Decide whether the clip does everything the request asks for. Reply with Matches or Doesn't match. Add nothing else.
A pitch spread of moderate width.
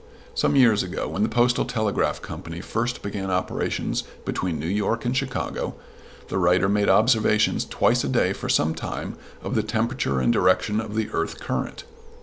Matches